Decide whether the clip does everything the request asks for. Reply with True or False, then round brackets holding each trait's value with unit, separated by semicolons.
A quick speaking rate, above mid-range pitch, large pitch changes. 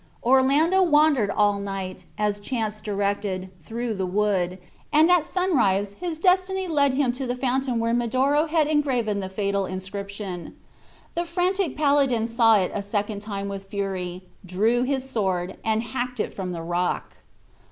False (155 wpm; 225 Hz; 6.0 semitones)